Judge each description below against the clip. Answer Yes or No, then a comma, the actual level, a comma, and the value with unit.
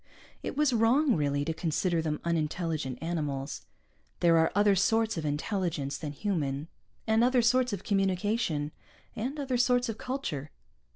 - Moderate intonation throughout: No, wide, 7.0 semitones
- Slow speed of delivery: No, average, 150 wpm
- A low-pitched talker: No, medium, 180 Hz